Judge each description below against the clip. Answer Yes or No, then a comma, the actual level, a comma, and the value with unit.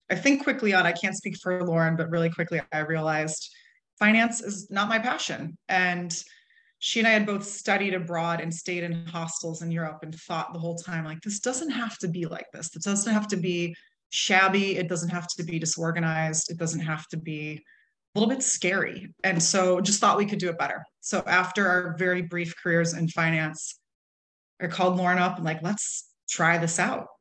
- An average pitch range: Yes, average, 3.3 semitones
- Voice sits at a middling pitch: Yes, medium, 180 Hz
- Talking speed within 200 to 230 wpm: Yes, fast, 205 wpm